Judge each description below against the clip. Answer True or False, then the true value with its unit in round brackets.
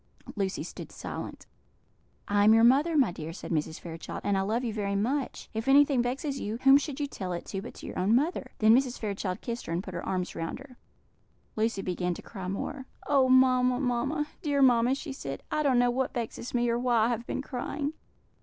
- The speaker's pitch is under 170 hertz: False (240 Hz)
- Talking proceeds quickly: True (220 wpm)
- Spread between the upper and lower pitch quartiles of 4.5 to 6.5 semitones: True (5.2 semitones)